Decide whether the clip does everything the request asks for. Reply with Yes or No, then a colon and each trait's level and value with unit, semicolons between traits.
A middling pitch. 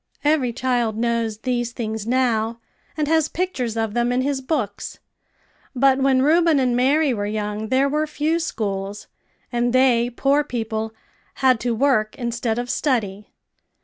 No: high, 245 Hz